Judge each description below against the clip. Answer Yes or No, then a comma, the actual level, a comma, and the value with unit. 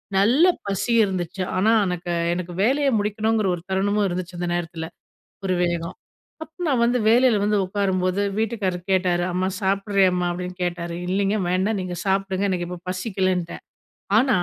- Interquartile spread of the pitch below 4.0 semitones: Yes, narrow, 2.6 semitones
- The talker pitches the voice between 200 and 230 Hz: No, high, 190 Hz